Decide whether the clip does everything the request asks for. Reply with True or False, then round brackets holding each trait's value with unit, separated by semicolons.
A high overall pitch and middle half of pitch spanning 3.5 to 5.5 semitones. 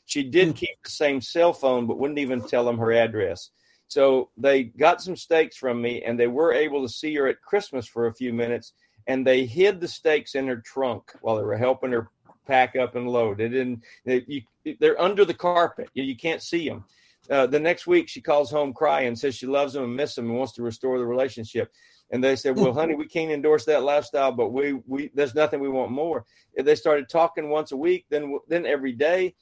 False (135 Hz; 4.1 semitones)